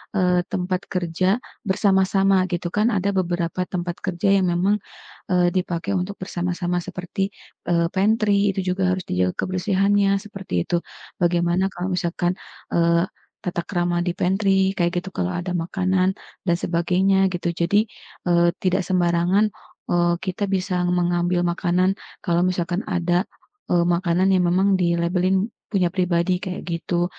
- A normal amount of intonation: No, narrow, 1.7 semitones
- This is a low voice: No, medium, 180 Hz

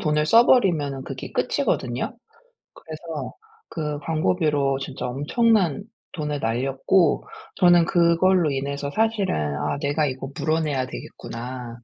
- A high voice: No, medium, 150 Hz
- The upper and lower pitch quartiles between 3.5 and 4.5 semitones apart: Yes, average, 4.0 semitones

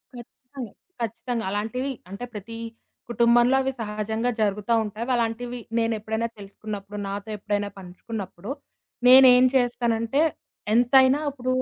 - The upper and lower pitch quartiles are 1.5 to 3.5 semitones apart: Yes, average, 2.9 semitones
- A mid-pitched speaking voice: No, high, 230 Hz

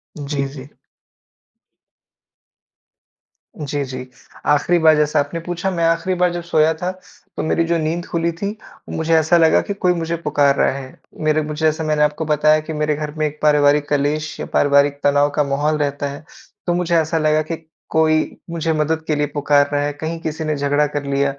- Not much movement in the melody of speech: Yes, narrow, 2.0 semitones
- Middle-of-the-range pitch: Yes, medium, 155 Hz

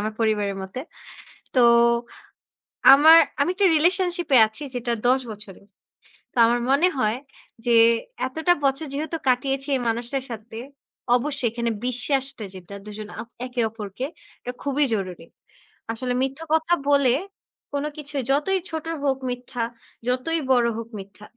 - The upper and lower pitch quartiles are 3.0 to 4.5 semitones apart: Yes, average, 4.2 semitones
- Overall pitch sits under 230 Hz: No, very high, 255 Hz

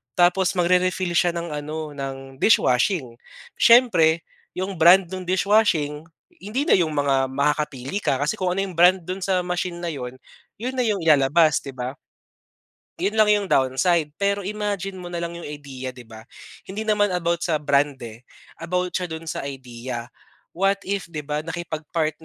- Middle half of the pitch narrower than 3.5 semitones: No, average, 4.6 semitones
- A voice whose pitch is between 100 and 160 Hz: No, medium, 170 Hz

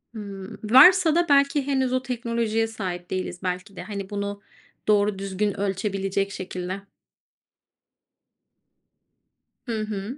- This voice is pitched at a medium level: No, high, 205 Hz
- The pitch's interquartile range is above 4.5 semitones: No, average, 3.6 semitones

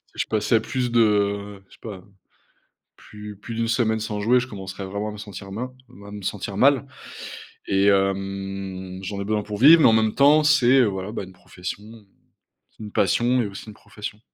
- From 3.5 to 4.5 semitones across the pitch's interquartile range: No, average, 2.8 semitones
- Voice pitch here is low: Yes, low, 105 Hz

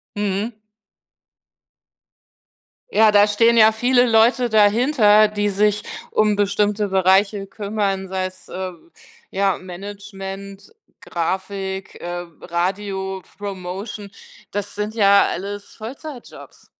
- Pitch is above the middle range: Yes, high, 205 Hz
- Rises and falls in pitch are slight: Yes, narrow, 1.9 semitones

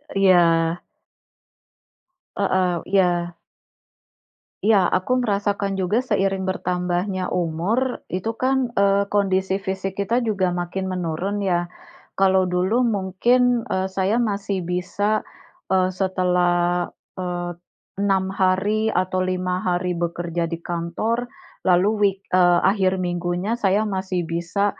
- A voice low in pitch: No, medium, 185 Hz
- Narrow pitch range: Yes, narrow, 2.1 semitones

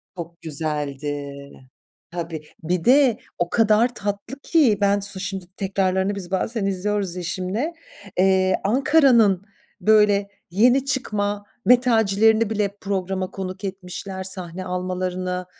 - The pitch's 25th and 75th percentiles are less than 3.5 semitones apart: Yes, average, 2.9 semitones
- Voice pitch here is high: Yes, high, 195 Hz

